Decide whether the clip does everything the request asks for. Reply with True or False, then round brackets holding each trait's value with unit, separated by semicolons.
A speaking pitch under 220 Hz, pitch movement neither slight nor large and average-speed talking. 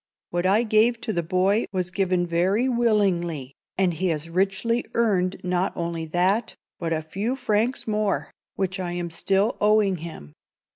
True (190 Hz; 3.7 semitones; 160 wpm)